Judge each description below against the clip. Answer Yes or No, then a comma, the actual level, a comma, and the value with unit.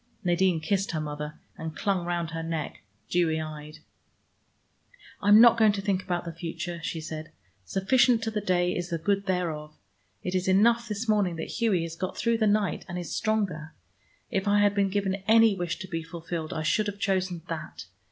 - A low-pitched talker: No, medium, 180 Hz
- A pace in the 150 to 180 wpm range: No, average, 195 wpm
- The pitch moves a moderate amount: Yes, average, 3.8 semitones